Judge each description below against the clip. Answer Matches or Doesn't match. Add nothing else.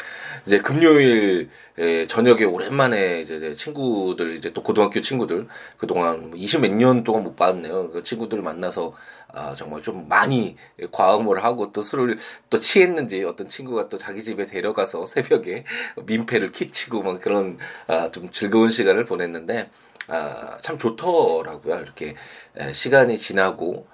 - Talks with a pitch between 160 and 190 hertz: Doesn't match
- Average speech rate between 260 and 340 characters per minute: Matches